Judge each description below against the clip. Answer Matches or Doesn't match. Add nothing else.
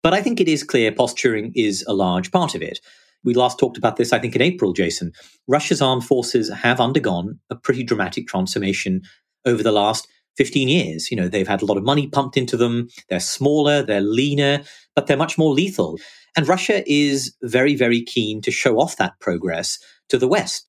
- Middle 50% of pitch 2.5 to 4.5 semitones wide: Doesn't match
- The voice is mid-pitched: Doesn't match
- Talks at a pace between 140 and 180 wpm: Doesn't match